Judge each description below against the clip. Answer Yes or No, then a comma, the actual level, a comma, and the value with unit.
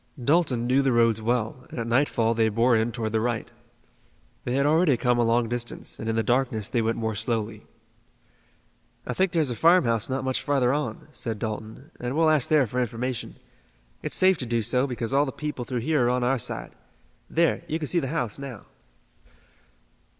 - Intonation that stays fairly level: No, average, 3.3 semitones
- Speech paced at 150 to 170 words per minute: No, average, 200 wpm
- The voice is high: No, low, 125 Hz